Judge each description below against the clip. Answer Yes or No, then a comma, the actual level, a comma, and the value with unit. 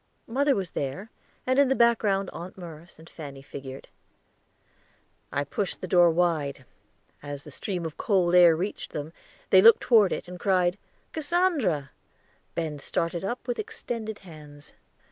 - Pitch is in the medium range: Yes, medium, 180 Hz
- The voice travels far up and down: Yes, wide, 5.9 semitones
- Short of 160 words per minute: Yes, average, 150 wpm